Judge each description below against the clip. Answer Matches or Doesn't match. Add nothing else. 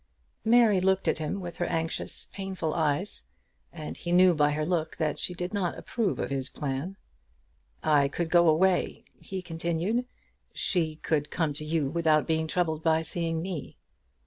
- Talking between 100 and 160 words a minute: Doesn't match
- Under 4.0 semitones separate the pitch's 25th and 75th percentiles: Matches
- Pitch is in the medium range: Matches